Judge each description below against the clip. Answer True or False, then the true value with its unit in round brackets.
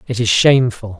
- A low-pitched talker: True (115 Hz)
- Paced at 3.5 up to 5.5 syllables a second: False (6.0 syllables/s)